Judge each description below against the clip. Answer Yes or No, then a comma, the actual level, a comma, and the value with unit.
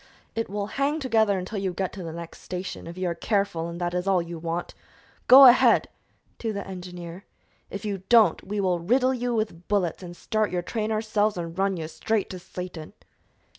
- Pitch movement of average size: Yes, average, 3.8 semitones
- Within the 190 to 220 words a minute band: Yes, fast, 205 wpm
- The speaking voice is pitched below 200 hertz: Yes, high, 190 Hz